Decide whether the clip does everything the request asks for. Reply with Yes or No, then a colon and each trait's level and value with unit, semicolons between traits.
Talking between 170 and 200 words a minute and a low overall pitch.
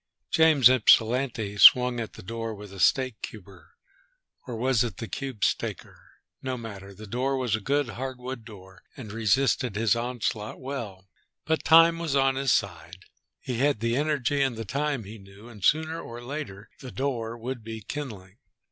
Yes: average, 175 wpm; low, 120 Hz